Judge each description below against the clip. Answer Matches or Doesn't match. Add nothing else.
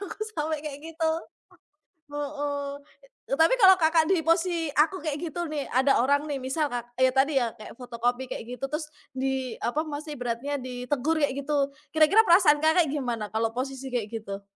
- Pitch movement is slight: Doesn't match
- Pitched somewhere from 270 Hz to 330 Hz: Matches